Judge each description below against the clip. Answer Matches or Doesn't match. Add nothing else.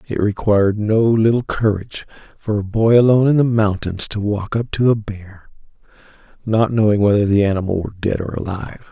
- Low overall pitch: Matches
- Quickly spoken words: Doesn't match